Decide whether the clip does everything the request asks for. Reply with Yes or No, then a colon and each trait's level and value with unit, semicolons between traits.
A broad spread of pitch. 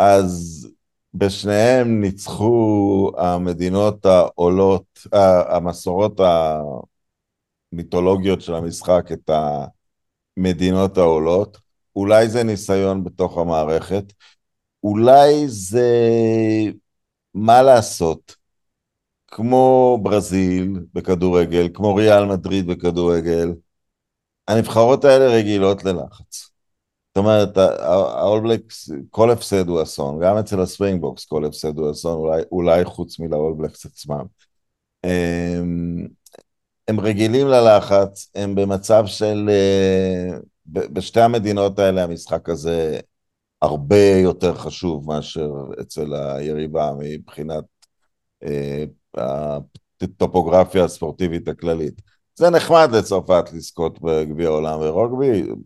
No: average, 3.7 semitones